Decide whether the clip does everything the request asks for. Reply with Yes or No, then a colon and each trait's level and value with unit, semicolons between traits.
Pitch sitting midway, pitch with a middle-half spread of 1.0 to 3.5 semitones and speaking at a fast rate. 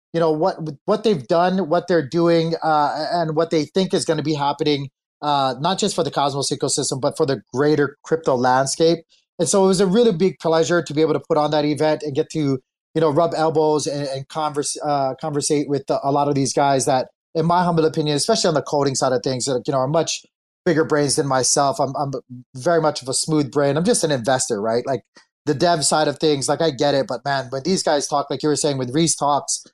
Yes: medium, 150 Hz; average, 2.7 semitones; fast, 250 wpm